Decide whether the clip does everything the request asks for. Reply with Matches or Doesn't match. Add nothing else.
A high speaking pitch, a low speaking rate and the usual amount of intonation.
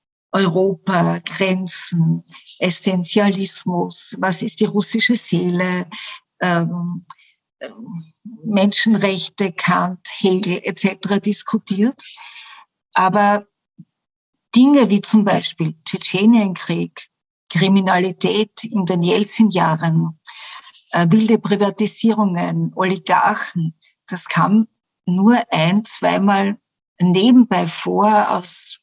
Matches